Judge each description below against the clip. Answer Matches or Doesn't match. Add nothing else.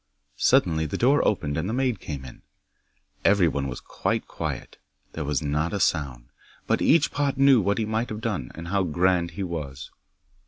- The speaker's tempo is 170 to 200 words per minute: Matches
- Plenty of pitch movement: Matches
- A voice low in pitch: Matches